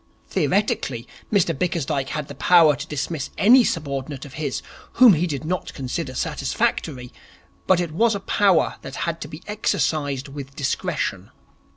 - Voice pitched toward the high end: No, medium, 155 Hz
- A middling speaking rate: Yes, average, 155 wpm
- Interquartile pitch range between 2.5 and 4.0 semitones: No, average, 4.5 semitones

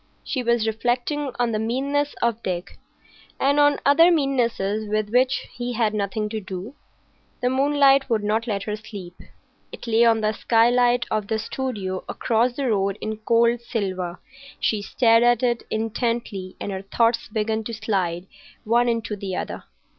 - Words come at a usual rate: Yes, average, 165 wpm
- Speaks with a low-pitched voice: No, high, 225 Hz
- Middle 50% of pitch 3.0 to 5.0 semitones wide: No, narrow, 2.6 semitones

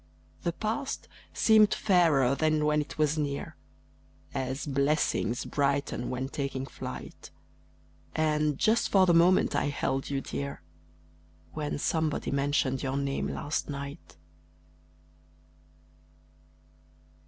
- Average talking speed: No, slow, 110 wpm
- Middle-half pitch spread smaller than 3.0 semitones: Yes, narrow, 2.5 semitones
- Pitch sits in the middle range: Yes, medium, 145 Hz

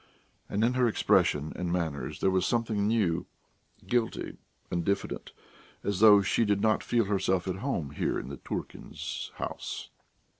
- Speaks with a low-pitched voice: Yes, low, 100 Hz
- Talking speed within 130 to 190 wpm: Yes, average, 155 wpm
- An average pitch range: Yes, average, 3.9 semitones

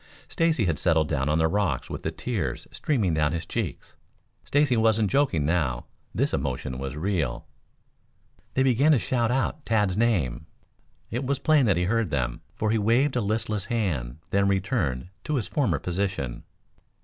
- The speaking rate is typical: Yes, average, 170 wpm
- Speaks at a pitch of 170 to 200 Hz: No, low, 100 Hz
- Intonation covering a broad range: Yes, wide, 7.4 semitones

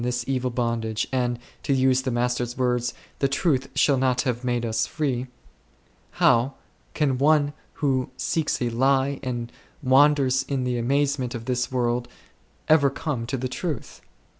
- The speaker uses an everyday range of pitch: No, narrow, 2.1 semitones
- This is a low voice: Yes, low, 130 Hz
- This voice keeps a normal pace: Yes, average, 160 wpm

